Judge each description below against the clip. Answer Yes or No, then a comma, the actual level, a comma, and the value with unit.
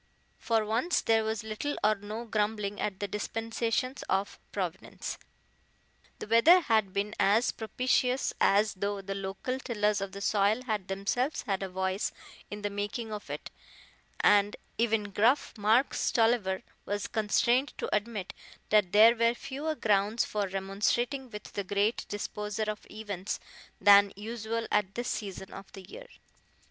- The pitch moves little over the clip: Yes, narrow, 2.3 semitones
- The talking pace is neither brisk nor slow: Yes, average, 150 wpm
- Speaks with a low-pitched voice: No, high, 210 Hz